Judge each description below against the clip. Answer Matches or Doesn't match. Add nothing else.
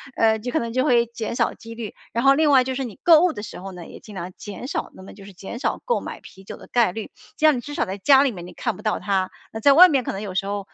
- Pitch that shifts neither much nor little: Matches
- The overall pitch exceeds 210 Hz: Matches